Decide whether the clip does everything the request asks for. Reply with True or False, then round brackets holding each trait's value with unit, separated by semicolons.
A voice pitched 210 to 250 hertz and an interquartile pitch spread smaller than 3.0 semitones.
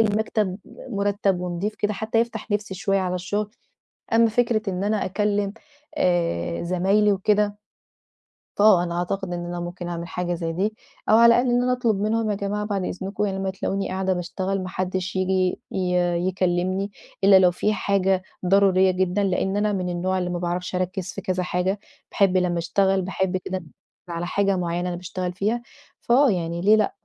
False (190 Hz; 2.4 semitones)